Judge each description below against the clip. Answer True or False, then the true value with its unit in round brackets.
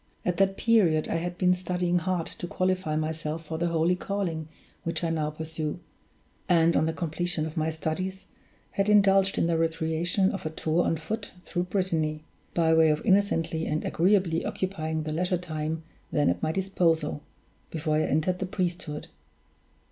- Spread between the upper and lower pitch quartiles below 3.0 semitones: True (2.5 semitones)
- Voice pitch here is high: False (165 Hz)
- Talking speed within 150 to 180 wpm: True (170 wpm)